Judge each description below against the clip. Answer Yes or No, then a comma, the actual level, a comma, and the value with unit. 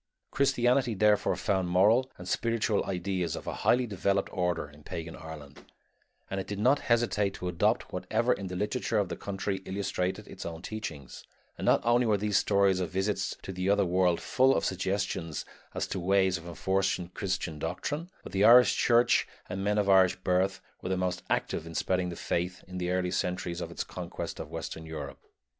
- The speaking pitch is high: No, very low, 95 Hz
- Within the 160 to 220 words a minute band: Yes, average, 190 wpm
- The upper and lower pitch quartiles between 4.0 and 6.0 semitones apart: No, narrow, 2.6 semitones